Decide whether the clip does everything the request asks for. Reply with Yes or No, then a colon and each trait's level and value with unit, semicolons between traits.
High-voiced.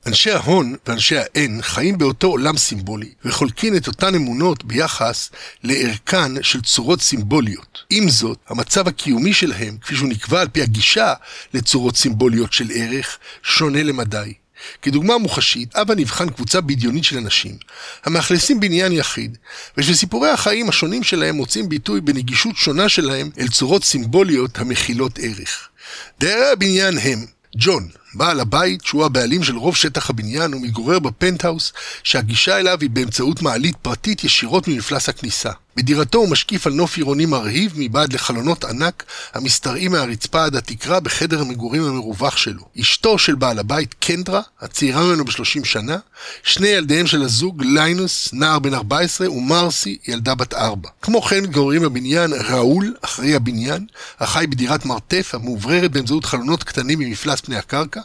No: medium, 145 Hz